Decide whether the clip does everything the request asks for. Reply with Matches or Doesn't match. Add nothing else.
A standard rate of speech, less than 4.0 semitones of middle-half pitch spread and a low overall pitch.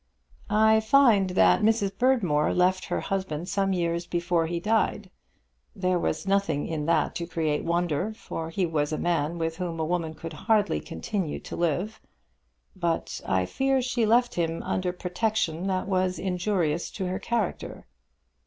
Doesn't match